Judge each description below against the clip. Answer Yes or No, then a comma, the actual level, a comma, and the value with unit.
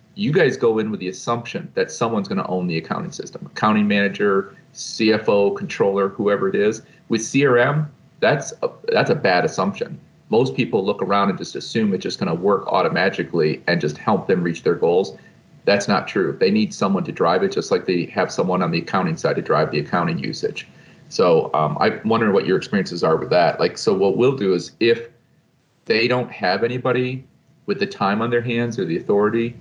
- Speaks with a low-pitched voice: Yes, low, 120 Hz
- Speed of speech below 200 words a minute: No, fast, 205 wpm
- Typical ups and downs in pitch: No, wide, 7.8 semitones